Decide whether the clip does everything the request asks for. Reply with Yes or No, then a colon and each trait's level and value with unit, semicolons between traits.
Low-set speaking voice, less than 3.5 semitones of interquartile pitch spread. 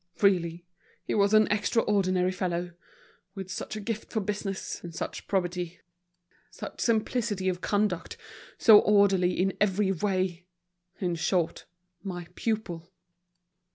No: high, 190 Hz; average, 2.7 semitones